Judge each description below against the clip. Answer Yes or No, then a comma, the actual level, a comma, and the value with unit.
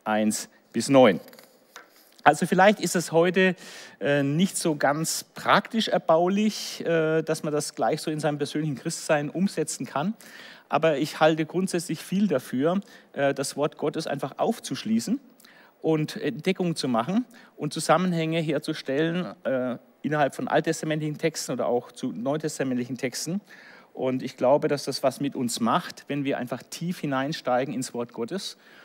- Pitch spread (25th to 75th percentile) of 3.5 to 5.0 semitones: Yes, average, 4.6 semitones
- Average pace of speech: Yes, average, 150 wpm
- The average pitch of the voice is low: No, medium, 160 Hz